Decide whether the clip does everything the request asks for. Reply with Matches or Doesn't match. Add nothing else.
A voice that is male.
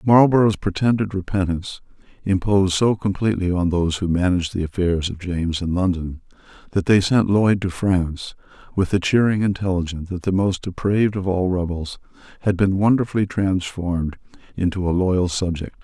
Matches